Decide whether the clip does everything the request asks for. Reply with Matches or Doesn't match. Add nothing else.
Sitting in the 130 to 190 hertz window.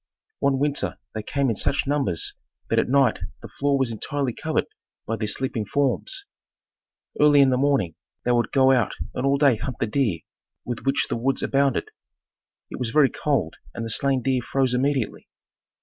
Matches